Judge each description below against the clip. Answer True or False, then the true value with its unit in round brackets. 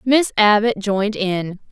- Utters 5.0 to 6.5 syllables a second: False (4.1 syllables/s)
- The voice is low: False (210 Hz)